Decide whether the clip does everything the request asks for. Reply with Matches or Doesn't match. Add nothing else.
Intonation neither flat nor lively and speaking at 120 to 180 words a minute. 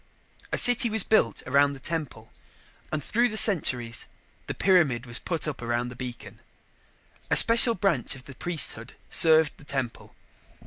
Doesn't match